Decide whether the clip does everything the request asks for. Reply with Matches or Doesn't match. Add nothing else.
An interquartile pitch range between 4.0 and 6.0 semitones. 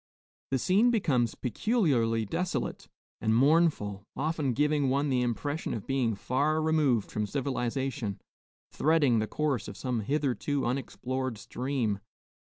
Matches